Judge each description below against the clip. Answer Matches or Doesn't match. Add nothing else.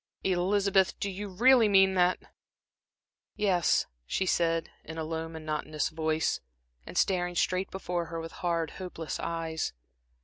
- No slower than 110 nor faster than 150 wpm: Matches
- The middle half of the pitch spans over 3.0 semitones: Doesn't match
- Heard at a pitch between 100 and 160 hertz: Doesn't match